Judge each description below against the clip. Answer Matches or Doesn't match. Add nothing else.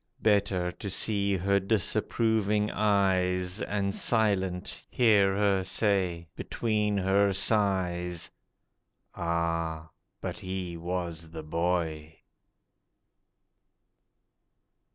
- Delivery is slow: Matches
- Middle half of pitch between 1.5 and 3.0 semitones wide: Matches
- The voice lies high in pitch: Doesn't match